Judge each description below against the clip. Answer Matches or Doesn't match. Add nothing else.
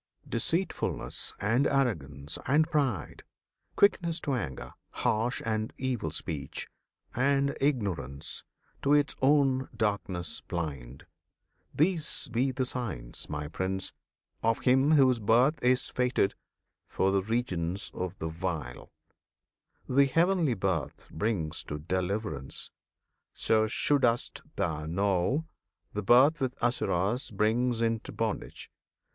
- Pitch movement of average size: Doesn't match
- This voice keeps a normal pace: Doesn't match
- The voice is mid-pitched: Doesn't match